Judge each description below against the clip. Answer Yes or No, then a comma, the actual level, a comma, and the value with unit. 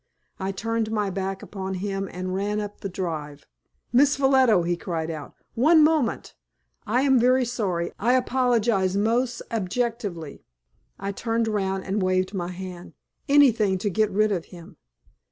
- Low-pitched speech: No, high, 205 Hz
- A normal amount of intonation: Yes, average, 4.2 semitones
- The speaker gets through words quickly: No, average, 155 wpm